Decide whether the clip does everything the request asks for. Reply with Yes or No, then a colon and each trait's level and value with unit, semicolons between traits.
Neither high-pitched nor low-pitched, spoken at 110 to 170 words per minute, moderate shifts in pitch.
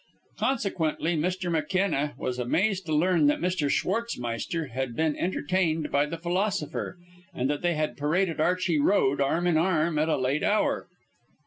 Yes: medium, 165 Hz; average, 155 wpm; average, 3.7 semitones